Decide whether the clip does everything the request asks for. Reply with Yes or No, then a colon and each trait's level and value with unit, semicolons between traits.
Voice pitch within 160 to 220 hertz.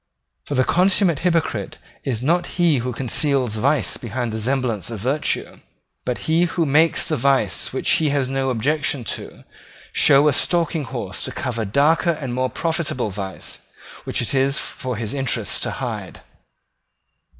No: low, 135 Hz